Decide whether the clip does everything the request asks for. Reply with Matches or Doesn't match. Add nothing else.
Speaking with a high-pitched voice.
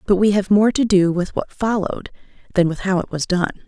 Matches